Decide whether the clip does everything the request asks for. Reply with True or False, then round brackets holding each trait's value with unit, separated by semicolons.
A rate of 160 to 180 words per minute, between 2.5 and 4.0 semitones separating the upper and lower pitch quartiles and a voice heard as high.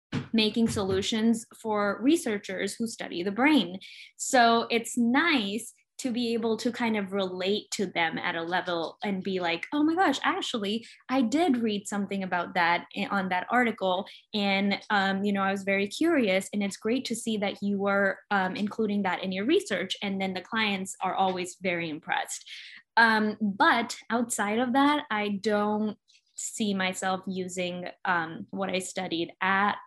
True (170 wpm; 3.4 semitones; 205 Hz)